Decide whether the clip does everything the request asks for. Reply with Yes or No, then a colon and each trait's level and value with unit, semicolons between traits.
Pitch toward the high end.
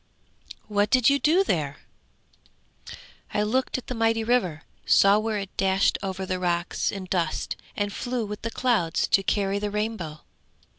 Yes: high, 205 Hz